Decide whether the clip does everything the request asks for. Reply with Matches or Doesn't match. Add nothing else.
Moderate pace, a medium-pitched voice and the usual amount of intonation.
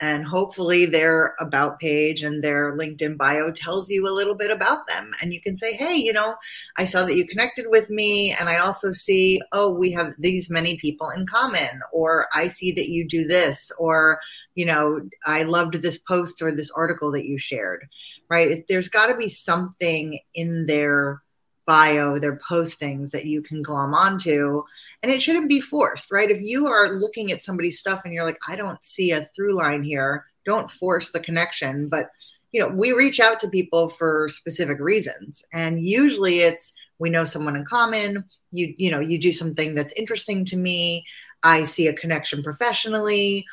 Matches